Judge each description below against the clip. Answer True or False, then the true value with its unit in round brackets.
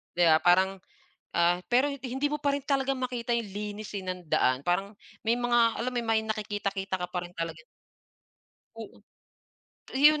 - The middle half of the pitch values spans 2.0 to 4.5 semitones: False (5.5 semitones)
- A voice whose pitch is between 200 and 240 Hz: True (215 Hz)